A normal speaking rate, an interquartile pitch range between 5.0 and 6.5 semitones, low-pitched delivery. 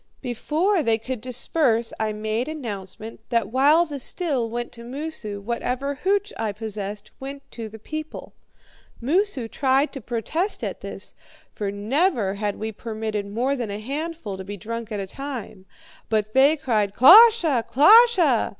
No: average, 155 wpm; wide, 5.4 semitones; high, 240 Hz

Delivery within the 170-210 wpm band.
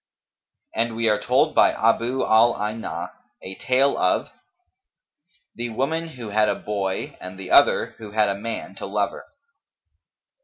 No: average, 155 wpm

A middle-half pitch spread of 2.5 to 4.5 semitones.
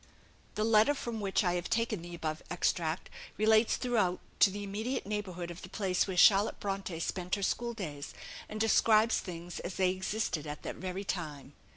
Yes: average, 3.6 semitones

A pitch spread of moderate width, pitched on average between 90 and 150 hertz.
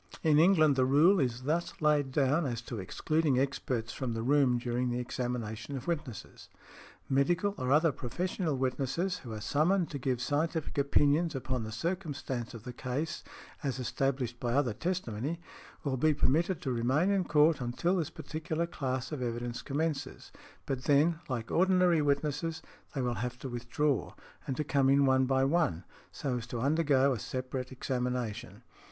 Yes: average, 4.0 semitones; low, 135 Hz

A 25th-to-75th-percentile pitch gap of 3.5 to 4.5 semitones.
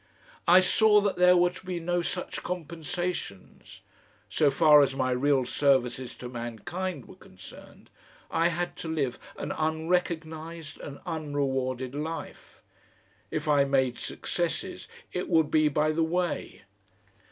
Yes: average, 4.2 semitones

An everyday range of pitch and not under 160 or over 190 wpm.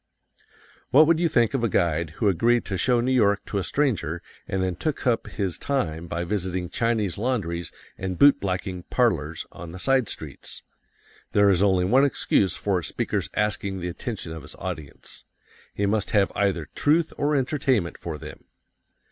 No: wide, 5.8 semitones; average, 180 wpm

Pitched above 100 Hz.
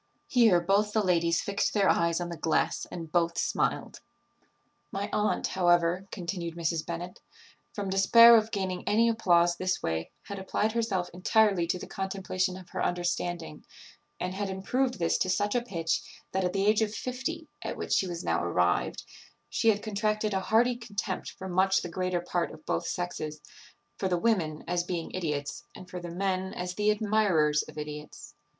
Yes: medium, 185 Hz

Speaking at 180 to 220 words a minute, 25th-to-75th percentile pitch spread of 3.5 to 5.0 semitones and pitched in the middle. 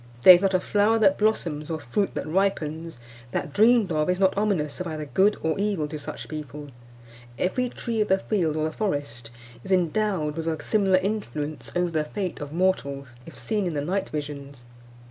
Yes: average, 200 wpm; average, 4.7 semitones; medium, 170 Hz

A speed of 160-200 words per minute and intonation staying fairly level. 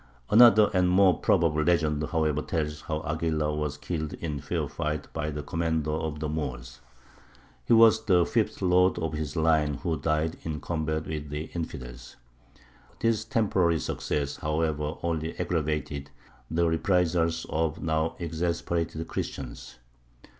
No: average, 140 wpm; narrow, 2.1 semitones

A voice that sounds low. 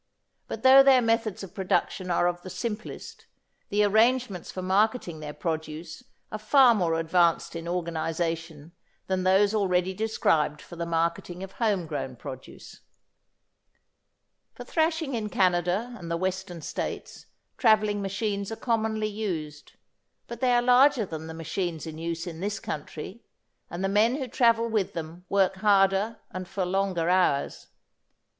No: high, 190 Hz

